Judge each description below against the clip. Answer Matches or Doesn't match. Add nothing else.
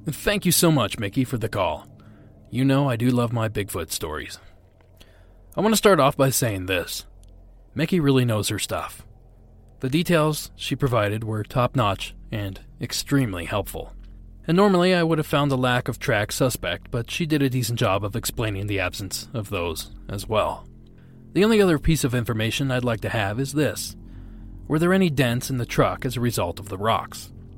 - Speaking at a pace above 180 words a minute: Matches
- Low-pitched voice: Matches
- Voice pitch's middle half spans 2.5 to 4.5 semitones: Doesn't match